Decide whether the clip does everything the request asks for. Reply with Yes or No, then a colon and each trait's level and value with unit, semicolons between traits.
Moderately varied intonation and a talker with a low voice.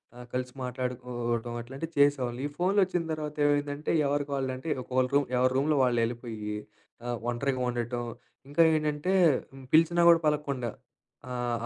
Yes: average, 3.6 semitones; low, 130 Hz